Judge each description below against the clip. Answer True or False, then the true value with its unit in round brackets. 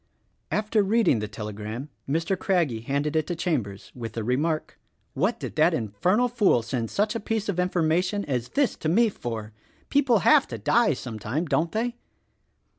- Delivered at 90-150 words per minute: False (170 wpm)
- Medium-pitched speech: True (160 Hz)